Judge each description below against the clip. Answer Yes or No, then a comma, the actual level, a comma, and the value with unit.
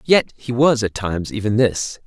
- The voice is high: No, low, 115 Hz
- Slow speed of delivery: No, fast, 205 wpm